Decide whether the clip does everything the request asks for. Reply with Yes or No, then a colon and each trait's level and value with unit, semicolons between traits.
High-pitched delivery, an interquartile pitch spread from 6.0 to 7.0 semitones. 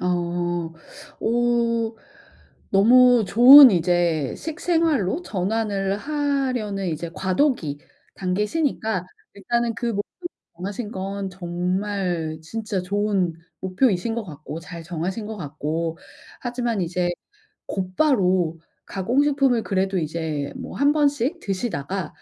No: high, 200 Hz; average, 5.2 semitones